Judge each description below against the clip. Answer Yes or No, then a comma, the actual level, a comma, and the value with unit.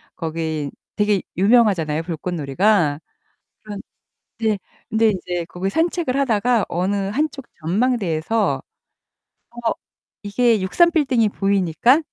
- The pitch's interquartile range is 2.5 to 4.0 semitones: No, average, 5.3 semitones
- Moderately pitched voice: No, high, 205 Hz